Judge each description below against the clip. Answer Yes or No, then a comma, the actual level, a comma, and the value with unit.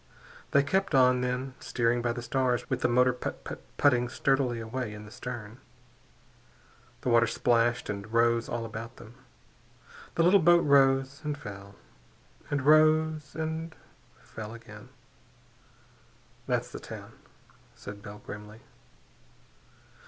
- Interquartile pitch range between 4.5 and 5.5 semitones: No, average, 3.4 semitones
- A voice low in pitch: Yes, low, 125 Hz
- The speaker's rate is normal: No, slow, 130 wpm